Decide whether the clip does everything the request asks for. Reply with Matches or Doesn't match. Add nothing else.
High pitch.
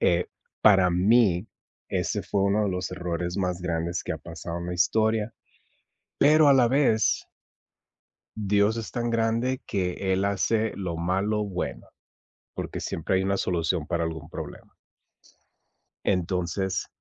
Doesn't match